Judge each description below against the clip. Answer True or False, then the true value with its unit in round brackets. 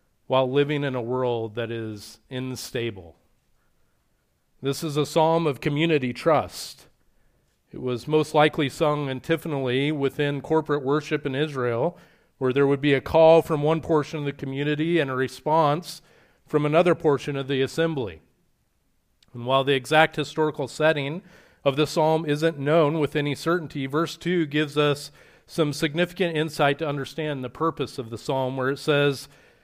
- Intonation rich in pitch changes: False (2.8 semitones)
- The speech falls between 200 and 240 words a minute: False (160 wpm)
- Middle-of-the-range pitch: True (145 Hz)